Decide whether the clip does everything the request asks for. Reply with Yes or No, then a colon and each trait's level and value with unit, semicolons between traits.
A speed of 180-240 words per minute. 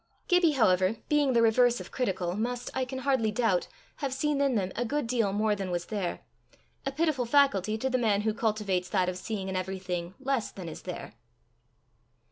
Yes: average, 195 wpm